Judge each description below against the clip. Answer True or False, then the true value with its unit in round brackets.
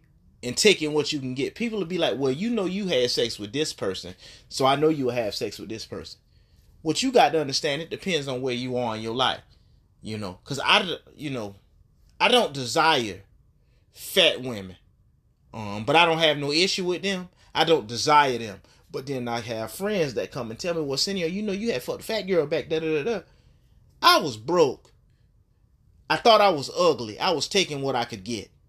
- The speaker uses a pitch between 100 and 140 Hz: True (135 Hz)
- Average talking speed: False (220 wpm)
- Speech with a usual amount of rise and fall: False (7.4 semitones)